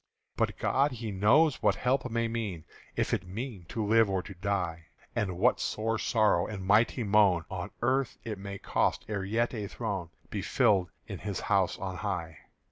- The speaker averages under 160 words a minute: No, average, 185 wpm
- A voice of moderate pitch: No, low, 105 Hz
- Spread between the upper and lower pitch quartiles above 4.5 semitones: No, average, 3.3 semitones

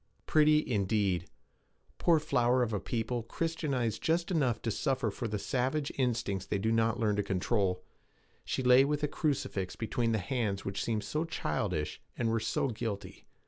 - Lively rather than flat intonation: No, average, 4.8 semitones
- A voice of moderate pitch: No, low, 115 Hz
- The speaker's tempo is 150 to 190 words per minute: Yes, average, 170 wpm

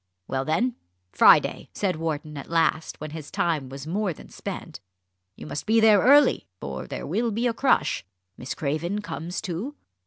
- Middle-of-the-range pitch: Yes, medium, 165 Hz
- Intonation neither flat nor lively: No, wide, 6.3 semitones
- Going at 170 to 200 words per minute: Yes, average, 175 wpm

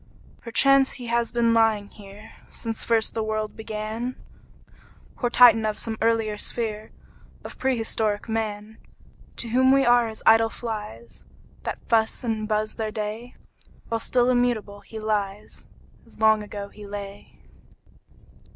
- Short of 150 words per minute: Yes, average, 140 wpm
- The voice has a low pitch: No, high, 220 Hz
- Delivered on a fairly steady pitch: Yes, narrow, 1.7 semitones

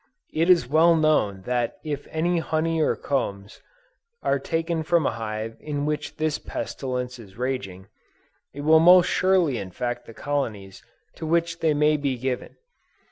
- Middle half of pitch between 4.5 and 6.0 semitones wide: Yes, average, 4.8 semitones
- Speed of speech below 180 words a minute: Yes, average, 155 wpm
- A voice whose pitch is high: No, medium, 145 Hz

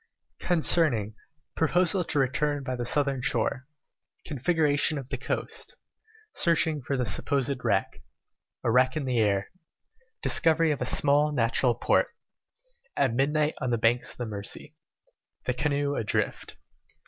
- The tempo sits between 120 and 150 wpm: Yes, average, 140 wpm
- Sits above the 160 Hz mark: No, low, 135 Hz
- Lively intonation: No, average, 3.4 semitones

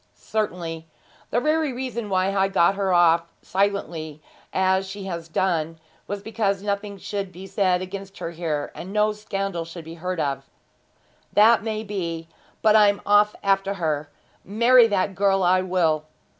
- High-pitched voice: Yes, high, 195 Hz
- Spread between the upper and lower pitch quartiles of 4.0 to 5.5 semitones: No, average, 3.2 semitones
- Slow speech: No, average, 165 wpm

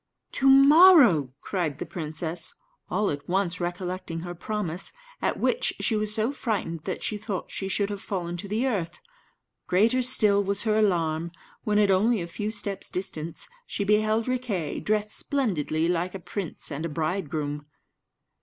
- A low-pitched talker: No, high, 195 Hz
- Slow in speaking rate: No, average, 165 wpm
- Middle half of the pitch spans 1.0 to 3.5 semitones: No, average, 4.2 semitones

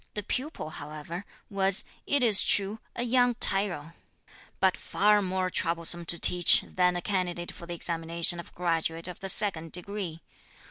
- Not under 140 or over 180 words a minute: Yes, average, 155 wpm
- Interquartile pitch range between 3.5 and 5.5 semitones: No, average, 3.1 semitones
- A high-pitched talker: No, medium, 180 Hz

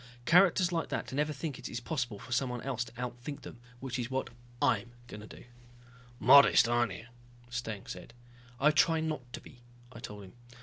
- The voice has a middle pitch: No, low, 125 Hz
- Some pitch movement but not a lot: Yes, average, 3.6 semitones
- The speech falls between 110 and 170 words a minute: No, average, 185 wpm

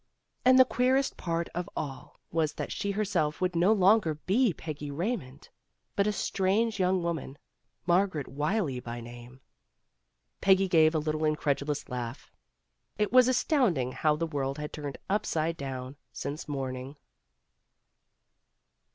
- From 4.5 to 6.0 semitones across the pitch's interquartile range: Yes, wide, 5.6 semitones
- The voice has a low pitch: No, medium, 160 Hz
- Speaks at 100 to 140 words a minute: Yes, slow, 135 wpm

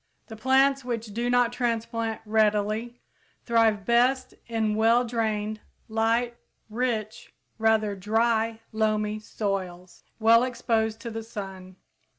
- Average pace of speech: No, slow, 115 wpm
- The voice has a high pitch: Yes, high, 225 Hz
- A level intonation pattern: Yes, narrow, 1.7 semitones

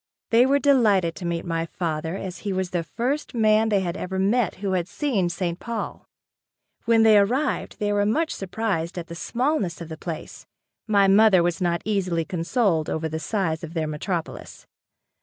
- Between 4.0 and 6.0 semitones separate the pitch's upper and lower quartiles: Yes, average, 4.6 semitones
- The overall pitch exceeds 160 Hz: Yes, high, 190 Hz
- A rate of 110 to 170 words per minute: No, average, 185 wpm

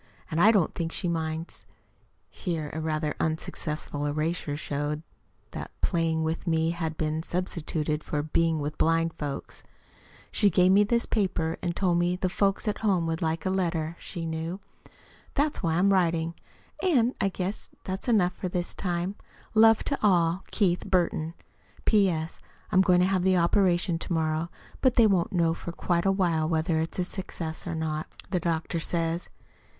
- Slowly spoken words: No, average, 170 wpm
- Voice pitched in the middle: Yes, medium, 170 Hz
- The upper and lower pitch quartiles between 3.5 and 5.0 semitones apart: No, average, 2.7 semitones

